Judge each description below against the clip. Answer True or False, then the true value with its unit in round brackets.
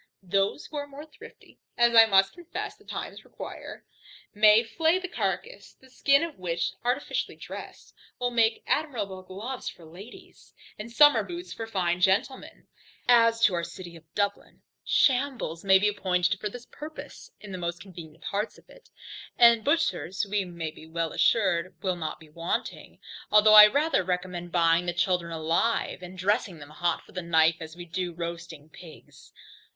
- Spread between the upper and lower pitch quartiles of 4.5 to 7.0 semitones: True (5.4 semitones)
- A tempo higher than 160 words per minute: True (170 wpm)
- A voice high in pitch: True (195 Hz)